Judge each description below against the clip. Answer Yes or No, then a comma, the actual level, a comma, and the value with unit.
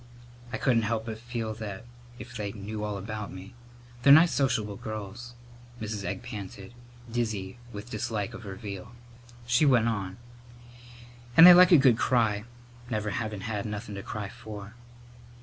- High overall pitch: No, low, 110 Hz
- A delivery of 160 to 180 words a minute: Yes, average, 165 wpm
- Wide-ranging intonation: No, average, 2.8 semitones